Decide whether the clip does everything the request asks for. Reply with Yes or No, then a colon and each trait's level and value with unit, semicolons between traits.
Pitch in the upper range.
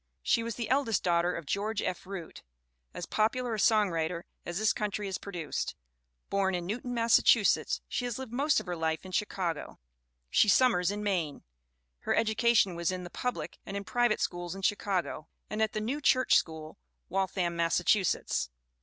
Yes: high, 195 Hz